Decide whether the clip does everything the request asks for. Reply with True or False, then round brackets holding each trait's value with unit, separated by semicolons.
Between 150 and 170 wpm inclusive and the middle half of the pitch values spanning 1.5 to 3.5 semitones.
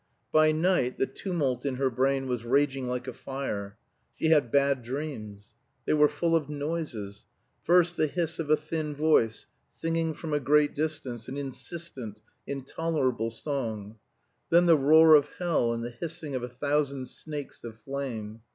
False (165 wpm; 4.1 semitones)